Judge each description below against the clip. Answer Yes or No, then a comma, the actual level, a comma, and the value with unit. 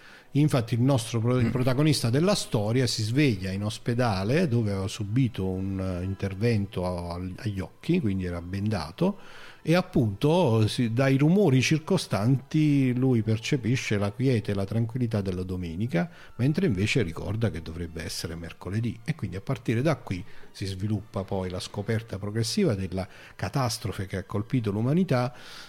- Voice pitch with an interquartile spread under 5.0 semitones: No, wide, 5.4 semitones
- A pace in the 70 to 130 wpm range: No, average, 140 wpm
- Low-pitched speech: Yes, low, 115 Hz